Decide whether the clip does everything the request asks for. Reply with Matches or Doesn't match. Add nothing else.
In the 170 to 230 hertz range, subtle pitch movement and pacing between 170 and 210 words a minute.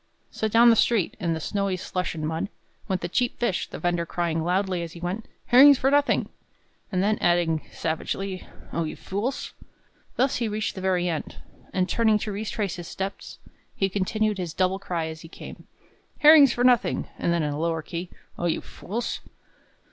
Doesn't match